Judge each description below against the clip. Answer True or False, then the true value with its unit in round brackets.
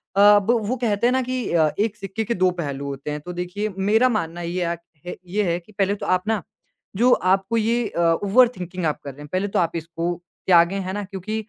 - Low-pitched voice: False (190 Hz)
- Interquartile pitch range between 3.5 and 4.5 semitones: True (3.9 semitones)